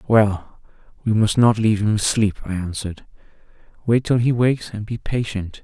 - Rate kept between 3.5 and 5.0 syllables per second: No, 5.2 syllables/s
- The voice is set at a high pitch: No, low, 110 Hz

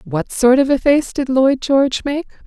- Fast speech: Yes, fast, 220 wpm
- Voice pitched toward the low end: No, very high, 265 Hz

